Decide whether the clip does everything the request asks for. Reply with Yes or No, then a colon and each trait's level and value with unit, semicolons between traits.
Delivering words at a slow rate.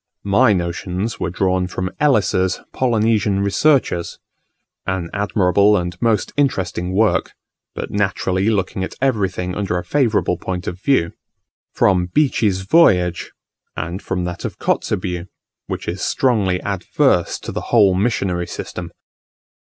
Yes: slow, 130 wpm